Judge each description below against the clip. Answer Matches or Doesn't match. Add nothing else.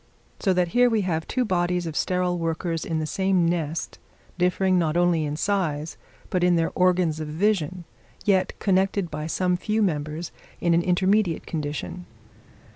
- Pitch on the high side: Doesn't match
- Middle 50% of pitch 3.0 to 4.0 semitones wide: Doesn't match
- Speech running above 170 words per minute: Doesn't match